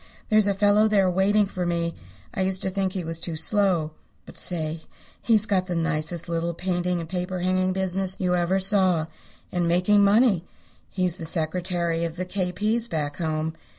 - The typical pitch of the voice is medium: Yes, medium, 180 Hz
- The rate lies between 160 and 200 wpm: Yes, average, 180 wpm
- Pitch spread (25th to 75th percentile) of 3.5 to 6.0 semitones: No, narrow, 2.5 semitones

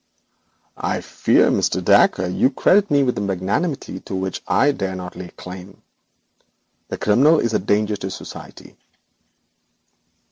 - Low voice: Yes, low, 100 Hz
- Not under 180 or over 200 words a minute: No, average, 140 wpm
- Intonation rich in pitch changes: Yes, wide, 6.2 semitones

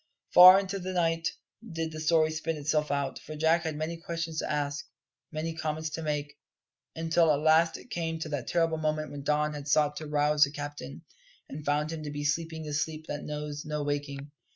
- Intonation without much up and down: Yes, narrow, 1.8 semitones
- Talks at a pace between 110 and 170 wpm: No, fast, 205 wpm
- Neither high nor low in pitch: Yes, medium, 155 Hz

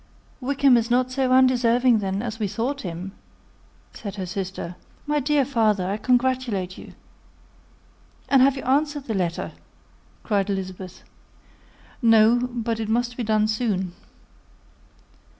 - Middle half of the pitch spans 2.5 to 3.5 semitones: No, average, 4.4 semitones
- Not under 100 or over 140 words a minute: Yes, slow, 135 wpm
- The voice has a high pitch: Yes, high, 230 Hz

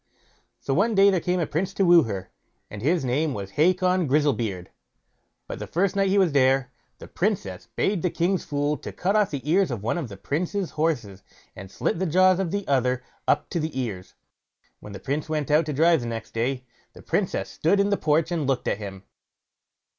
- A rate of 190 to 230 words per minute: Yes, fast, 205 wpm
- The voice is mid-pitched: Yes, medium, 150 Hz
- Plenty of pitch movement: Yes, wide, 6.4 semitones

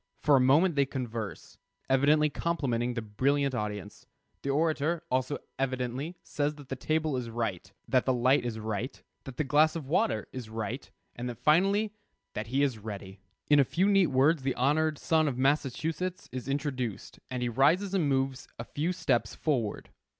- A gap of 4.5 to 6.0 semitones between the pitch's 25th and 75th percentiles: No, average, 3.9 semitones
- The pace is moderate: Yes, average, 175 wpm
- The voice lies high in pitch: No, low, 135 Hz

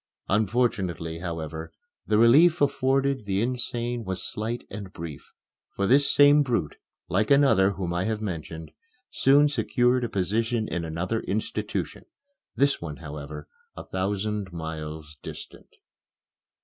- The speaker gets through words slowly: Yes, slow, 125 wpm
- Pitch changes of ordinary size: No, wide, 6.4 semitones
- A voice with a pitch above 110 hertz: No, low, 105 Hz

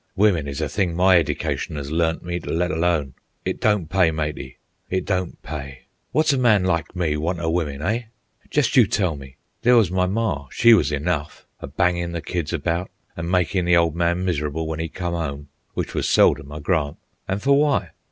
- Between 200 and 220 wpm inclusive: Yes, fast, 205 wpm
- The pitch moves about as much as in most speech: Yes, average, 3.4 semitones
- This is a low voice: Yes, very low, 85 Hz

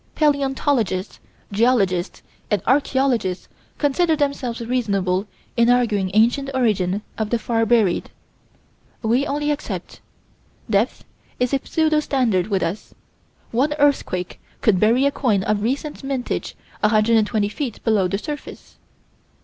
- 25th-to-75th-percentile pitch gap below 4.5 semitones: No, average, 5.0 semitones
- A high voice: Yes, high, 235 Hz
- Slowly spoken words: Yes, slow, 120 wpm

